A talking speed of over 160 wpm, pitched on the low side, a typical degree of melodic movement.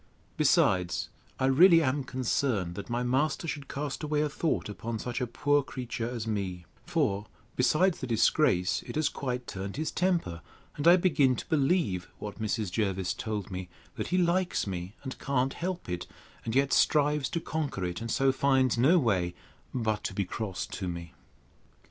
No: average, 180 wpm; low, 125 Hz; wide, 6.8 semitones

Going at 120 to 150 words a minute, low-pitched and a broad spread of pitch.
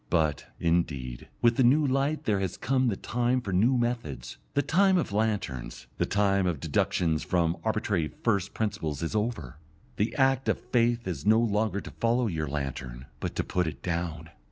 No: average, 180 wpm; low, 100 Hz; wide, 6.5 semitones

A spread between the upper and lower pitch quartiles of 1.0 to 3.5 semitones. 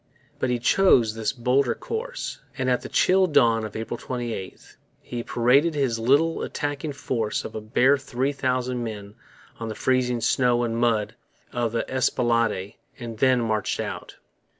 Yes: average, 2.8 semitones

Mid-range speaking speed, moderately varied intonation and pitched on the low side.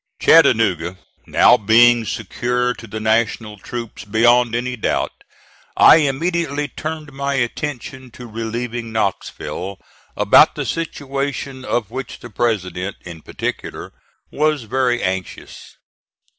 No: slow, 115 wpm; average, 3.7 semitones; low, 120 Hz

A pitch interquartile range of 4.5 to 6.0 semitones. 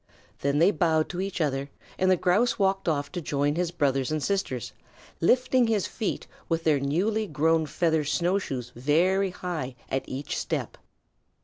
Yes: average, 5.0 semitones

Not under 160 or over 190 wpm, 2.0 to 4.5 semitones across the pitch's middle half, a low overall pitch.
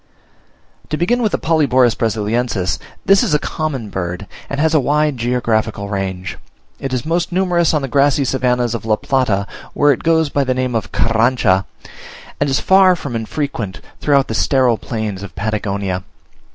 No: average, 170 wpm; wide, 5.6 semitones; low, 125 Hz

